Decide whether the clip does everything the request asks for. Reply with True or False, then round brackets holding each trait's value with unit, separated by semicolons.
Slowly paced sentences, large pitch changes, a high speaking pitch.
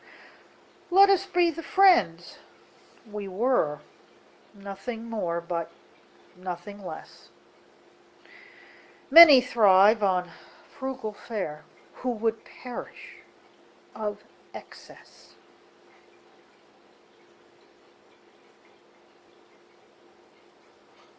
True (55 wpm; 5.9 semitones; 215 Hz)